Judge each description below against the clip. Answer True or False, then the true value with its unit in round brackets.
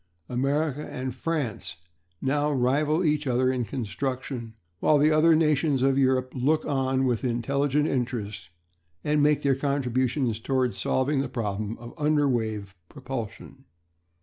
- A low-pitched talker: True (130 Hz)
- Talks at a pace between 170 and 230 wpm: False (145 wpm)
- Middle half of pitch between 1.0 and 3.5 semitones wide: True (3.2 semitones)